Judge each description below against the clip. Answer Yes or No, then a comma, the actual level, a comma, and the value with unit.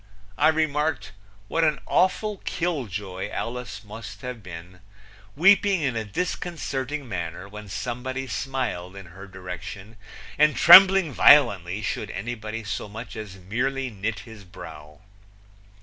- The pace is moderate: No, slow, 130 wpm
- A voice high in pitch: No, low, 115 Hz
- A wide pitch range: Yes, wide, 6.7 semitones